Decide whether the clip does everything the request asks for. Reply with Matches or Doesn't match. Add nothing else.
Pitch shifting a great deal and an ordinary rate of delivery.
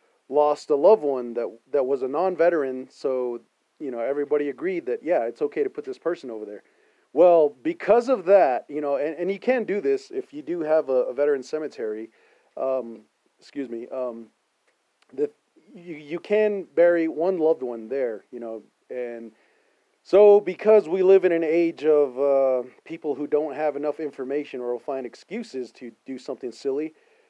Matches